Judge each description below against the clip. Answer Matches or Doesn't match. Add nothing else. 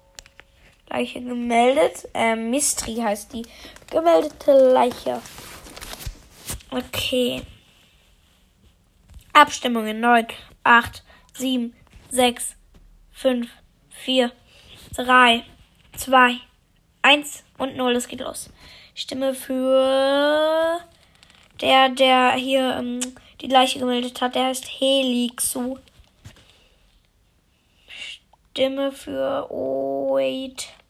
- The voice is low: Doesn't match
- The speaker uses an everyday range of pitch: Doesn't match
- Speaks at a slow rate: Matches